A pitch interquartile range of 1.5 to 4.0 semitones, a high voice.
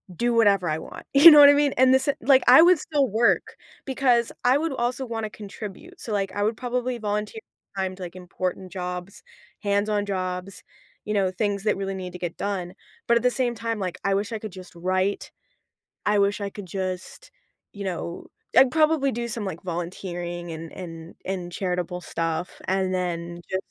No: average, 4.7 semitones; high, 200 Hz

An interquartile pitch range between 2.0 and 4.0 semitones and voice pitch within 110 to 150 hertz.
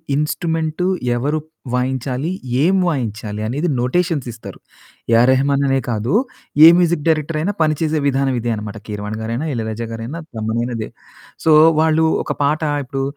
No: average, 5.3 semitones; low, 135 Hz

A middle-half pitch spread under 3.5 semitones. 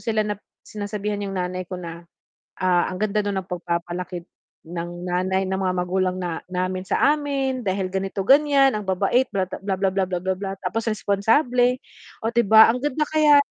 No: average, 3.8 semitones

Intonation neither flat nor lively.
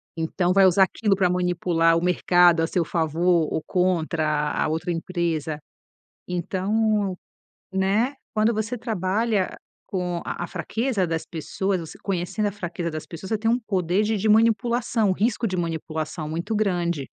Yes: average, 4.0 semitones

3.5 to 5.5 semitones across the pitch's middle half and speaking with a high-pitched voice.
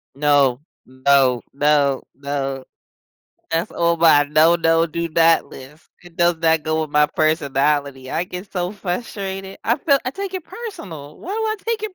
No: average, 4.6 semitones; medium, 160 Hz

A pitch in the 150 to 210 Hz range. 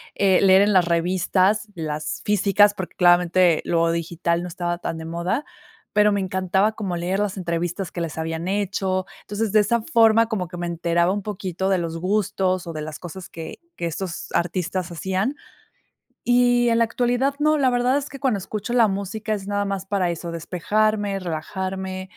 Yes: high, 190 Hz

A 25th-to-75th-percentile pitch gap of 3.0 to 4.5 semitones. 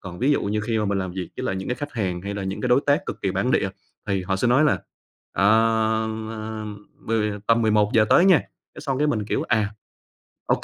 Yes: average, 4.1 semitones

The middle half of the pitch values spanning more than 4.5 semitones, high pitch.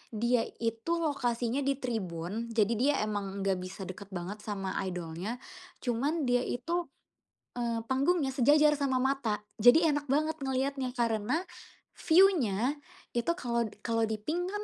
Yes: average, 5.0 semitones; high, 240 Hz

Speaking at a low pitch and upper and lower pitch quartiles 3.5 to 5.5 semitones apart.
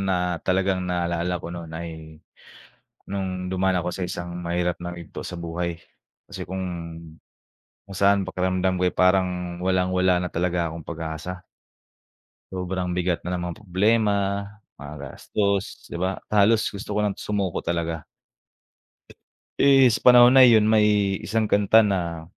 No: very low, 90 Hz; narrow, 2.4 semitones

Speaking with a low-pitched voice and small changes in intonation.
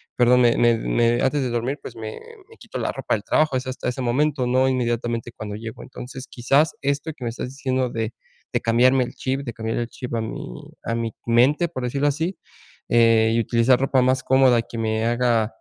Yes: low, 125 Hz; narrow, 2.2 semitones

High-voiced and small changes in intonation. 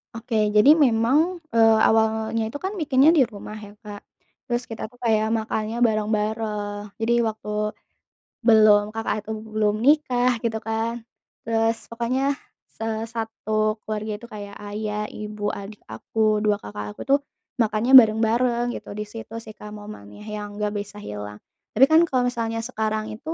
Yes: high, 220 Hz; narrow, 1.7 semitones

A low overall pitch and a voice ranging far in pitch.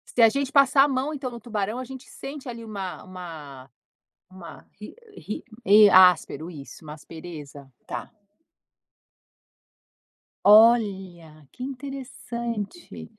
No: high, 210 Hz; wide, 7.1 semitones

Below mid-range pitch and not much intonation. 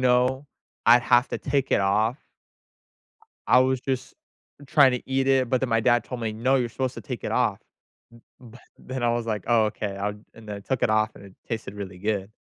No: low, 120 Hz; average, 3.1 semitones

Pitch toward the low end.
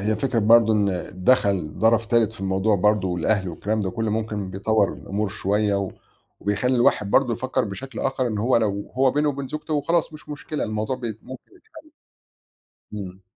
Yes: low, 110 Hz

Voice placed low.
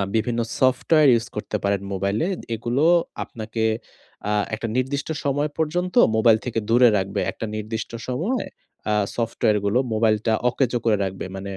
Yes: low, 115 Hz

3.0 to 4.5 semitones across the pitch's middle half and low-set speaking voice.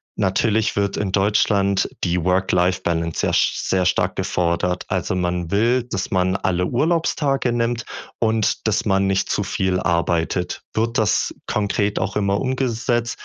Yes: average, 3.7 semitones; low, 100 Hz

